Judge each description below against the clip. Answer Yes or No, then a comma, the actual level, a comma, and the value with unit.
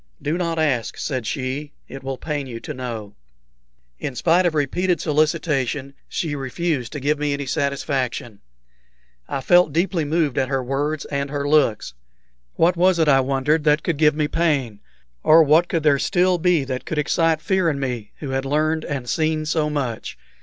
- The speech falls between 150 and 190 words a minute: Yes, average, 180 wpm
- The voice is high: No, medium, 150 Hz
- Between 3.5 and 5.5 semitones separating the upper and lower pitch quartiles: No, average, 3.1 semitones